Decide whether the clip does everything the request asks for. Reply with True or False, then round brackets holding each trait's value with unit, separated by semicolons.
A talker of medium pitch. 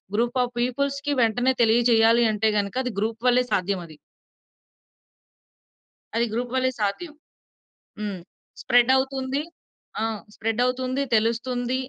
False (240 Hz)